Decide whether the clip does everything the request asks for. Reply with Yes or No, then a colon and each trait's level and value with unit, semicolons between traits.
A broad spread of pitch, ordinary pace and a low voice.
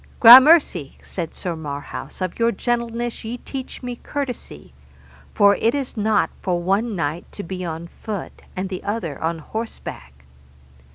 No: wide, 5.7 semitones; average, 150 wpm; high, 200 Hz